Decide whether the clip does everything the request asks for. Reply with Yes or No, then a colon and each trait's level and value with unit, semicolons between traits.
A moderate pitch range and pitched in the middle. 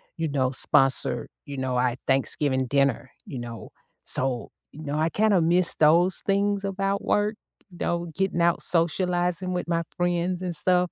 Yes: average, 4.9 semitones; medium, 170 Hz